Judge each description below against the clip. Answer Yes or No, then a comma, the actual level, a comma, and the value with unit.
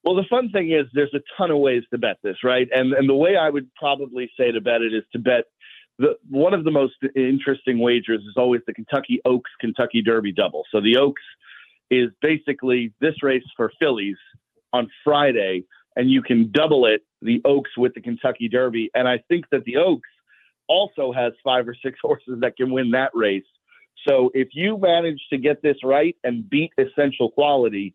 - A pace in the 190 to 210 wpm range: Yes, average, 200 wpm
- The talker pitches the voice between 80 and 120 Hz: No, low, 130 Hz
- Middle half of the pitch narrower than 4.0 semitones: Yes, average, 3.2 semitones